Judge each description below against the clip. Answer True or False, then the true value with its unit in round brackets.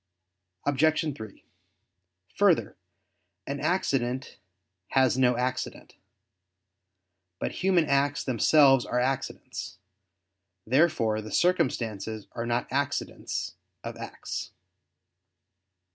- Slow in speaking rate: True (85 wpm)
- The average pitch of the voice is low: True (130 Hz)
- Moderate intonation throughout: True (3.5 semitones)